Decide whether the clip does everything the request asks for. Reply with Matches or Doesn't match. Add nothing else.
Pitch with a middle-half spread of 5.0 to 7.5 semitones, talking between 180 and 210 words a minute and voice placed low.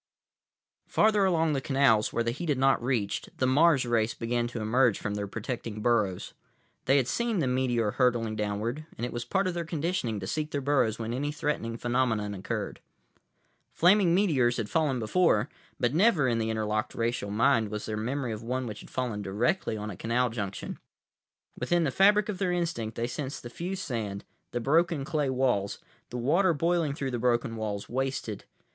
Matches